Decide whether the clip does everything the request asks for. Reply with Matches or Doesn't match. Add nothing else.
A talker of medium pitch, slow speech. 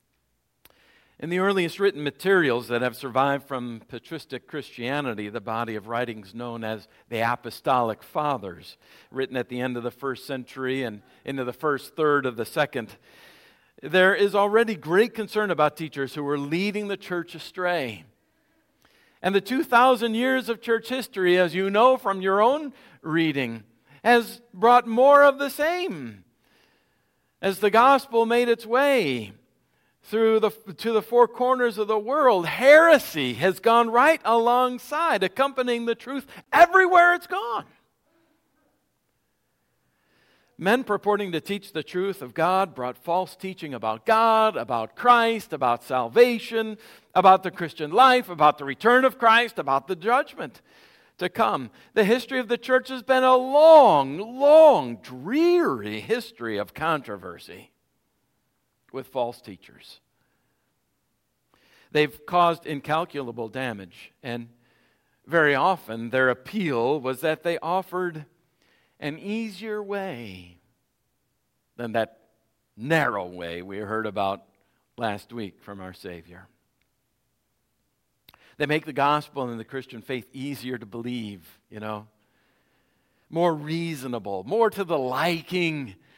Matches